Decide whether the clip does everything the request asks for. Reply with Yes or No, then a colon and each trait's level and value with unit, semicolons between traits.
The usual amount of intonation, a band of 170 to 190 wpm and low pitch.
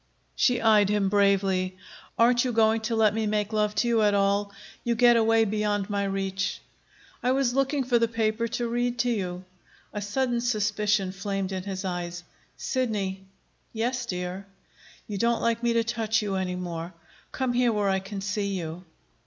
No: average, 3.2 semitones; average, 180 wpm; high, 210 Hz